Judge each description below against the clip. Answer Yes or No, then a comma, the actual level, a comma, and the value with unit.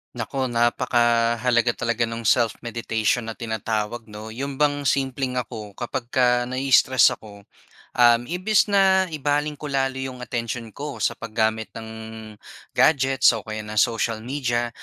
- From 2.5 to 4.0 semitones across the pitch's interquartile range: Yes, average, 2.9 semitones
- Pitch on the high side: No, low, 120 Hz